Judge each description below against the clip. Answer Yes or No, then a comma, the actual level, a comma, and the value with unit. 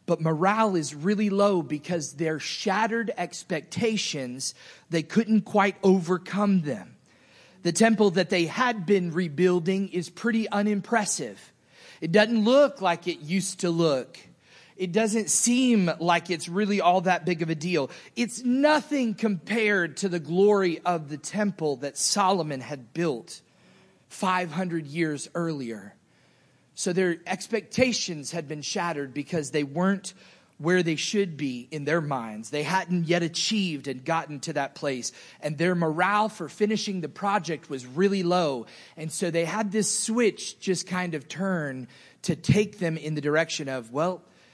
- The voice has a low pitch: No, medium, 180 Hz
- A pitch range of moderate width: Yes, average, 4.3 semitones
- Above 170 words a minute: No, average, 150 wpm